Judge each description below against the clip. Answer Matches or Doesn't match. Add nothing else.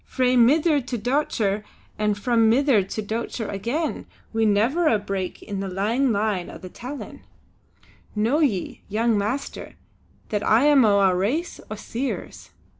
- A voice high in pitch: Matches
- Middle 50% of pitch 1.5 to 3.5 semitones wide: Doesn't match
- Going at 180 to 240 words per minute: Doesn't match